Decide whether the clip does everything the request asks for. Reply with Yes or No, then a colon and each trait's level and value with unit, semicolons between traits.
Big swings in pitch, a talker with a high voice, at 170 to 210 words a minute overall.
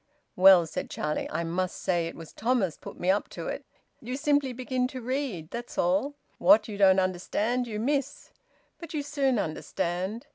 Yes: wide, 6.1 semitones; high, 215 Hz; average, 180 wpm